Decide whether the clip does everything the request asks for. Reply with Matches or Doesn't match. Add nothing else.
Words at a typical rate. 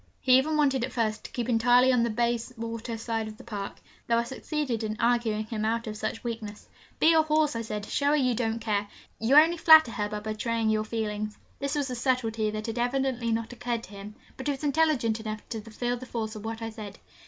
Doesn't match